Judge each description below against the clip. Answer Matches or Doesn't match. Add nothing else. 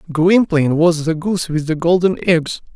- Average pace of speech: Matches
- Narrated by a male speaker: Matches